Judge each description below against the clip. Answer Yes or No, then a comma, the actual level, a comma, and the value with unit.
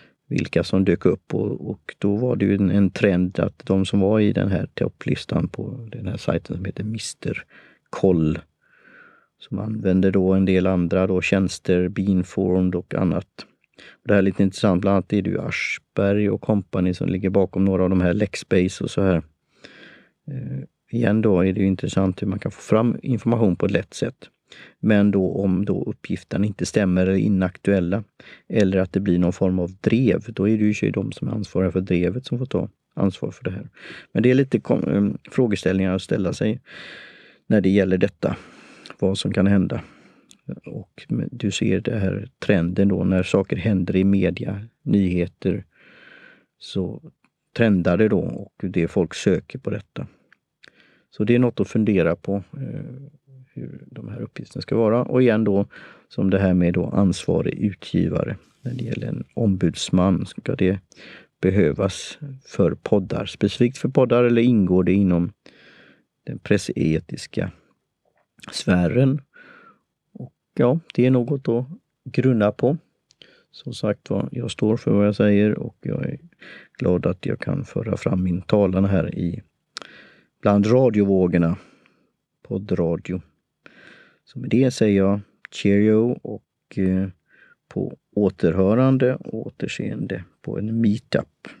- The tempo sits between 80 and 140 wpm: No, average, 160 wpm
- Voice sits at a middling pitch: No, low, 100 Hz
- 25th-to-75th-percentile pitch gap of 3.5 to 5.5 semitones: No, average, 3.1 semitones